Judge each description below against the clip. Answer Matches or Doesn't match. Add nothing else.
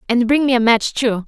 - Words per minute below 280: Doesn't match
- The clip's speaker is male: Doesn't match